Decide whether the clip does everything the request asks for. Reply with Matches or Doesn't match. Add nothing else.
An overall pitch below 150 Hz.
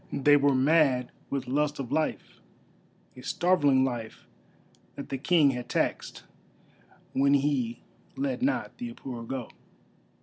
Matches